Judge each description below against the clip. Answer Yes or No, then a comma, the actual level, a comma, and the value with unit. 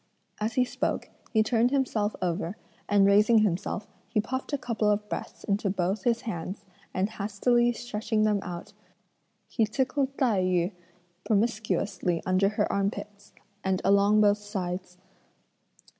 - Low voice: No, high, 210 Hz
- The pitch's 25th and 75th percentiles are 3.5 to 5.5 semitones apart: No, narrow, 2.5 semitones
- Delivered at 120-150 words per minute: Yes, average, 140 wpm